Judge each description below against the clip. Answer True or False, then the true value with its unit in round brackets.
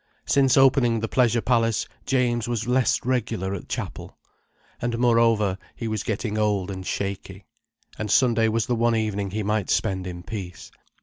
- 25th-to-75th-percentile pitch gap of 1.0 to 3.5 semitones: True (3.0 semitones)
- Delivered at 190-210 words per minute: False (165 wpm)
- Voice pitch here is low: True (110 Hz)